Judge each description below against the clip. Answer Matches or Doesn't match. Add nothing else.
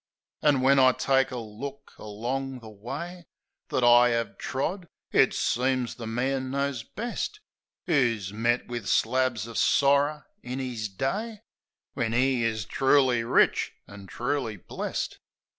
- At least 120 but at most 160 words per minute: Matches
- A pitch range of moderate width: Matches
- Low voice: Matches